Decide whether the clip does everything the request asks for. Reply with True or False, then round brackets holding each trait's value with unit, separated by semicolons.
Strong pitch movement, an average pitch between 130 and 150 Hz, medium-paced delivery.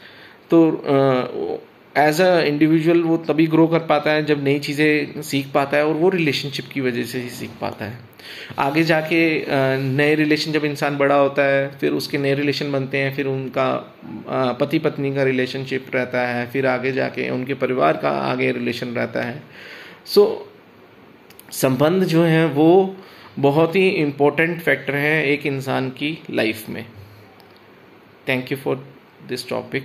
False (2.9 semitones; 140 Hz; 165 wpm)